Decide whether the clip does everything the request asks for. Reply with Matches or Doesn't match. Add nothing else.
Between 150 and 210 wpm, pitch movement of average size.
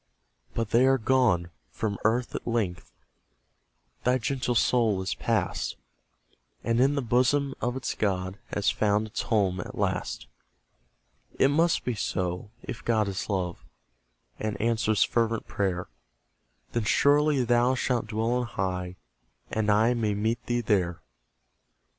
Doesn't match